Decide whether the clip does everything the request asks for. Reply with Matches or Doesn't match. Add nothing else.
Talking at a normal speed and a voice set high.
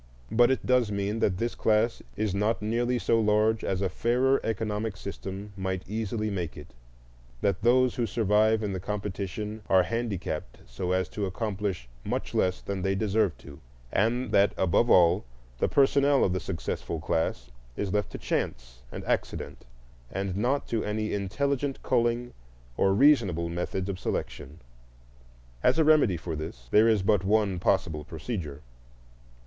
Doesn't match